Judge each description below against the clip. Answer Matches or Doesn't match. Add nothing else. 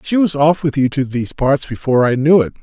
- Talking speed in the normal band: Doesn't match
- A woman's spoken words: Doesn't match